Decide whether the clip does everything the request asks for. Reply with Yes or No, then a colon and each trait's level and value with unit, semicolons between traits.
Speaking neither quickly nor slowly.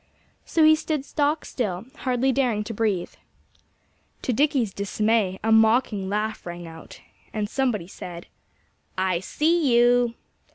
No: slow, 130 wpm